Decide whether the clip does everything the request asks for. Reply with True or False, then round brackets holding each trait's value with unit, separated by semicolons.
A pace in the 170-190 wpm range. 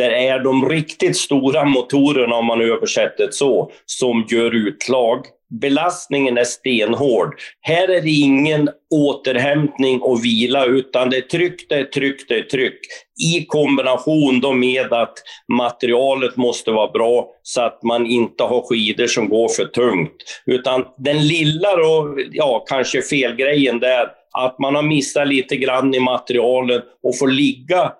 False (155 wpm)